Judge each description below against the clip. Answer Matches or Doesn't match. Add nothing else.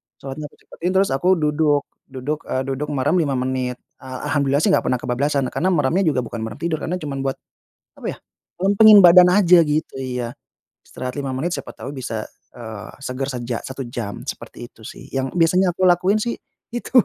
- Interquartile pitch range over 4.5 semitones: Matches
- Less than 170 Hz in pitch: Matches